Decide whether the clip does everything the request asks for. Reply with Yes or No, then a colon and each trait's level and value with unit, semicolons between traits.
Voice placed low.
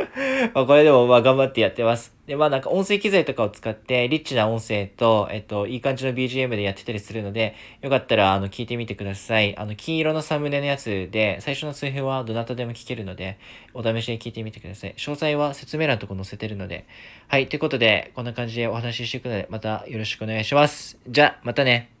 Yes: low, 120 Hz